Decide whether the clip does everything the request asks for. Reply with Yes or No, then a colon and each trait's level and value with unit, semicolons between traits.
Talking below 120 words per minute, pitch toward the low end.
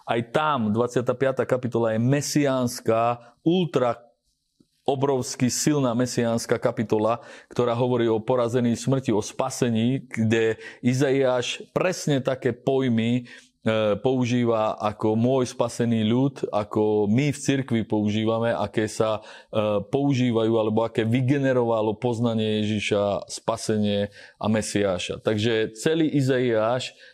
Yes: slow, 110 wpm; low, 120 Hz